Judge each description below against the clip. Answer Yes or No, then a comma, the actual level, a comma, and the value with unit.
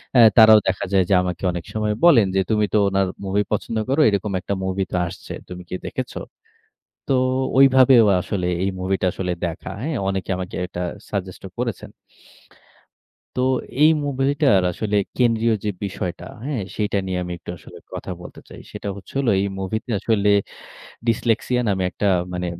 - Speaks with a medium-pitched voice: No, low, 100 Hz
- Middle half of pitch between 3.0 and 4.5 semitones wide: Yes, average, 3.7 semitones